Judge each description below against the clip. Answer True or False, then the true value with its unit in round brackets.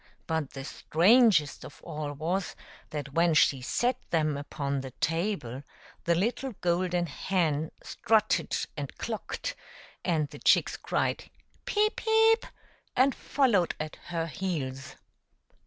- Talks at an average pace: False (130 wpm)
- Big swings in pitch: True (6.0 semitones)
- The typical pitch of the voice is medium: True (170 Hz)